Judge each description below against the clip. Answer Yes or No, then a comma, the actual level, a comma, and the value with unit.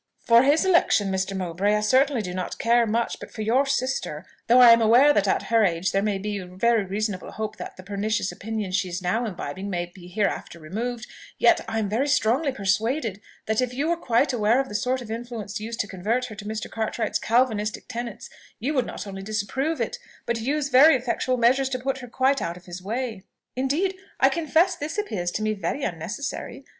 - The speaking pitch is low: No, high, 225 Hz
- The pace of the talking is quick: Yes, fast, 215 wpm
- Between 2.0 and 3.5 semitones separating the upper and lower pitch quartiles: No, average, 4.4 semitones